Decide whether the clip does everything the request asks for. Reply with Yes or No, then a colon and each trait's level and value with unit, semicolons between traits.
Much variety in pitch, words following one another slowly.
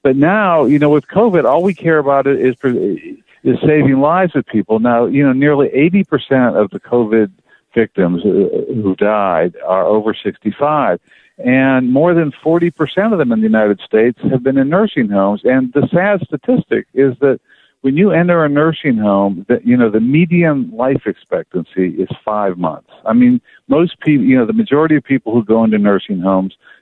No: wide, 6.5 semitones; average, 185 wpm